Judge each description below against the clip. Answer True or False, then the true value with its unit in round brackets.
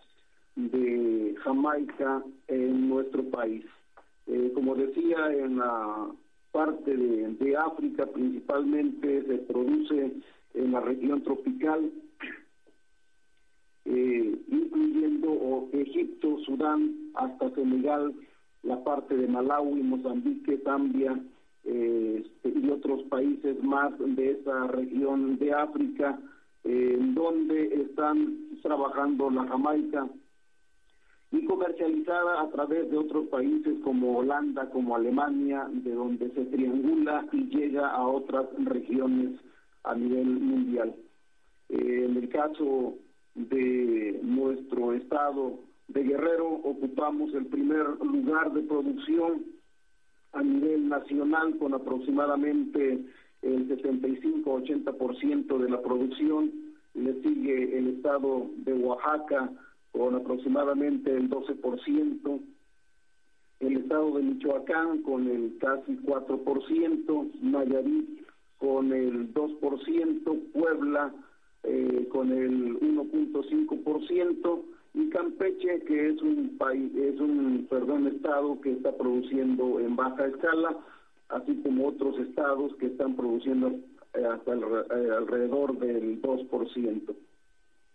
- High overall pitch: False (140 Hz)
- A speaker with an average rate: False (105 wpm)